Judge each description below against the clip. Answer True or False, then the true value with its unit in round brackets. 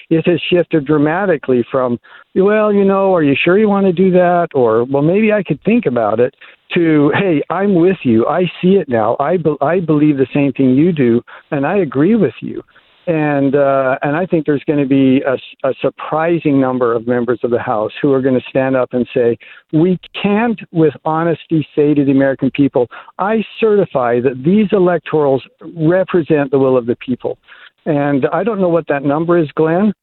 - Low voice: False (155 Hz)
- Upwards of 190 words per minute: True (205 wpm)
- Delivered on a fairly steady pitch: False (5.2 semitones)